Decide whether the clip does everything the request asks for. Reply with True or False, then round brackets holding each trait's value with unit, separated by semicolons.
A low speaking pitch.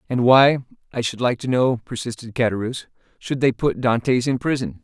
True (125 Hz)